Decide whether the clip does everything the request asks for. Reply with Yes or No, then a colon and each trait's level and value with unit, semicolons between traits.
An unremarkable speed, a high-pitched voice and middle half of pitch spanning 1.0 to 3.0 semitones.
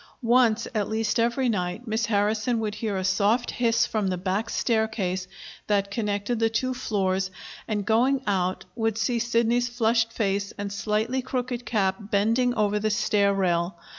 Yes: average, 165 wpm; high, 220 Hz; narrow, 2.6 semitones